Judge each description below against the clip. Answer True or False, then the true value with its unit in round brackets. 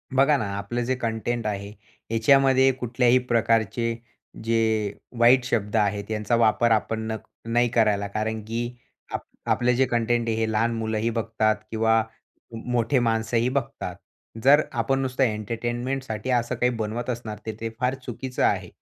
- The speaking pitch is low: True (115 Hz)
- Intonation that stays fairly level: True (1.8 semitones)